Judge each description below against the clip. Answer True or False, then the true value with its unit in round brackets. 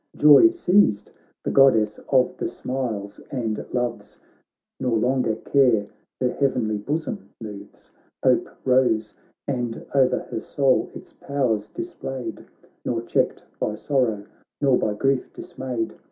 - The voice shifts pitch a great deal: False (3.6 semitones)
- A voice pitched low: True (125 Hz)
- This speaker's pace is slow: True (125 wpm)